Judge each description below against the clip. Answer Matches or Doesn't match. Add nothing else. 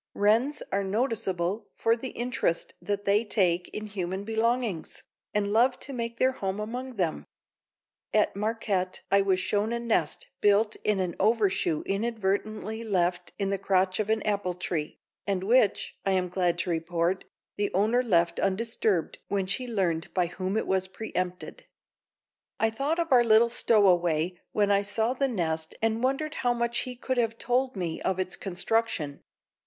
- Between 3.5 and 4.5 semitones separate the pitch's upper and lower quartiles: Matches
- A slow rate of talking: Doesn't match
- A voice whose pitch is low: Doesn't match